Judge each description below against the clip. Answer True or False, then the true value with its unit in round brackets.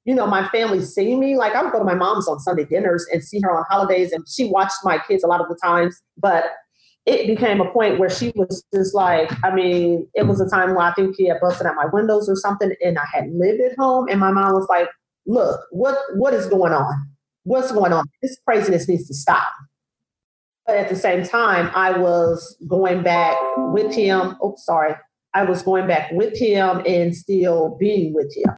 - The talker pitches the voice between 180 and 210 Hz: True (185 Hz)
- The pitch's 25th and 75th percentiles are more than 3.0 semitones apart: False (2.7 semitones)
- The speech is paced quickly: True (225 wpm)